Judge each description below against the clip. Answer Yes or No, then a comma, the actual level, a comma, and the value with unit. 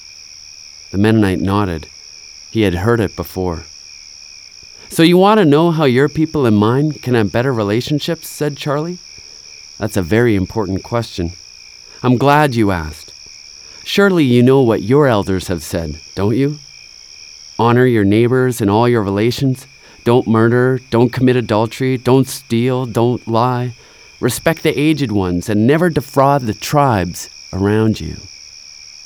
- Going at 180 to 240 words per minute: No, average, 145 wpm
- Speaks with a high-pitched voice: No, low, 115 Hz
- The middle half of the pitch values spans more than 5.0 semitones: Yes, wide, 5.4 semitones